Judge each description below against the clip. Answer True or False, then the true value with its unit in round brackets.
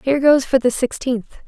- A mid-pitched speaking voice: False (260 Hz)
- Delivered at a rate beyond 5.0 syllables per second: False (4.9 syllables/s)